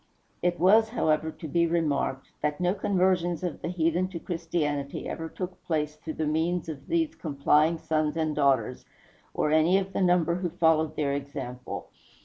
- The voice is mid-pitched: Yes, medium, 160 Hz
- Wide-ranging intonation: No, average, 2.9 semitones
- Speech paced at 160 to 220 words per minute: Yes, average, 170 wpm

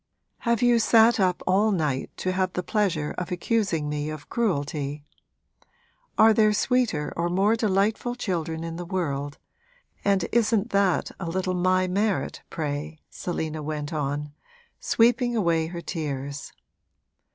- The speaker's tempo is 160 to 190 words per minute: No, average, 140 wpm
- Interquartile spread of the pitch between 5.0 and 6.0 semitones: Yes, wide, 5.5 semitones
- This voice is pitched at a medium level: Yes, medium, 180 Hz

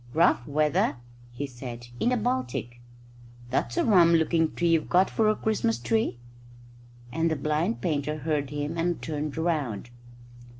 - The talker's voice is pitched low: No, medium, 155 Hz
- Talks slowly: No, average, 155 wpm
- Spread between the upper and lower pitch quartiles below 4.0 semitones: Yes, average, 3.5 semitones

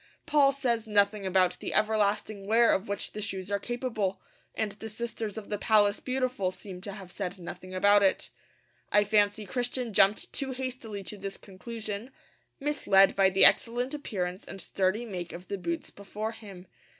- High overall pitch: Yes, high, 205 Hz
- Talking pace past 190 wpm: No, average, 175 wpm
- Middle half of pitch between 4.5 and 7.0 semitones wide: No, average, 3.0 semitones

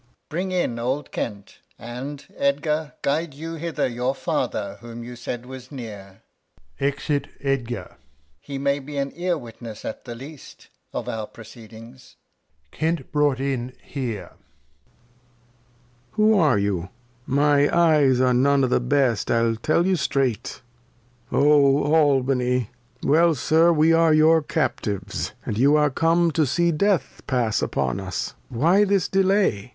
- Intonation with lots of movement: No, average, 4.6 semitones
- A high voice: No, medium, 140 Hz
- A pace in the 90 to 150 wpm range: Yes, average, 145 wpm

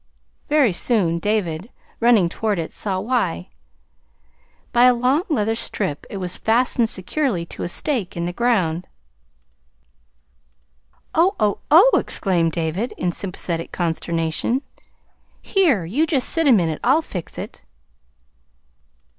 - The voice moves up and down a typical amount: No, wide, 6.5 semitones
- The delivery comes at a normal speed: No, slow, 125 wpm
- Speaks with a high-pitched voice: Yes, high, 205 Hz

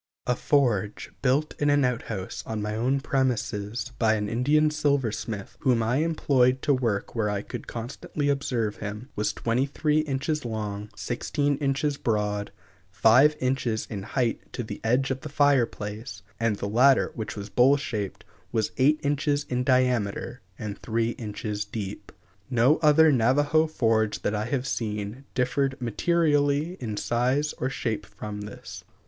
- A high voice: No, low, 125 Hz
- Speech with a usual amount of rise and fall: Yes, average, 4.7 semitones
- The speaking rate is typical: Yes, average, 155 wpm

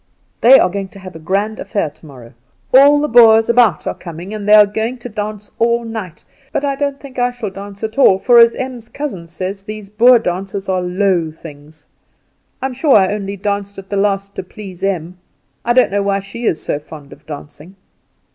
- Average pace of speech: No, fast, 210 wpm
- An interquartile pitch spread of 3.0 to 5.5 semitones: Yes, average, 4.0 semitones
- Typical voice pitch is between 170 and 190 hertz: No, high, 200 Hz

